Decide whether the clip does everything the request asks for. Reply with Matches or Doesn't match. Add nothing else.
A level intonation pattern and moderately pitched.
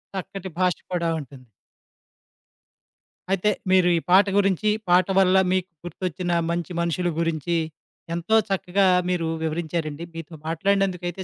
Matches